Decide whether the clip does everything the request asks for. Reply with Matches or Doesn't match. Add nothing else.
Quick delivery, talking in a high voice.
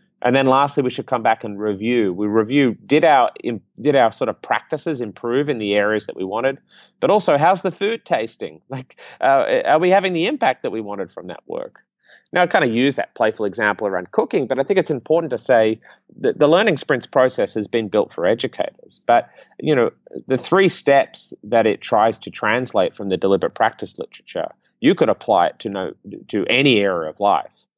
Doesn't match